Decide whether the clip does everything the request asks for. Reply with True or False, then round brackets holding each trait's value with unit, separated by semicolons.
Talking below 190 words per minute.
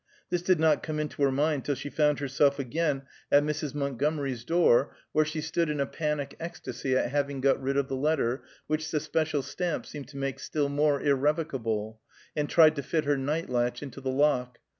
False (205 wpm)